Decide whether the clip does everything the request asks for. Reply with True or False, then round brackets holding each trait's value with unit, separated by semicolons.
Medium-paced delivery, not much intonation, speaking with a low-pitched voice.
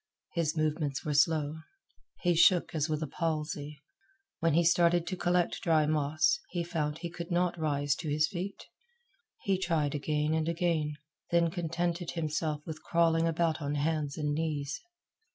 False (160 wpm; 2.2 semitones; 160 Hz)